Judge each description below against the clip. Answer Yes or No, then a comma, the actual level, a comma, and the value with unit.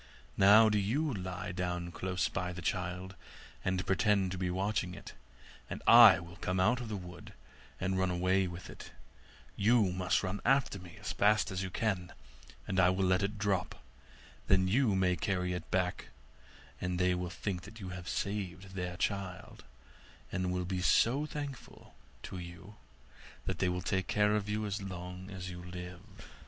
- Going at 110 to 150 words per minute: No, average, 175 wpm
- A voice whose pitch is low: Yes, very low, 95 Hz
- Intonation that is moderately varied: No, narrow, 2.1 semitones